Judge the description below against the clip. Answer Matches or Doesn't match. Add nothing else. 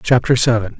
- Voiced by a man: Matches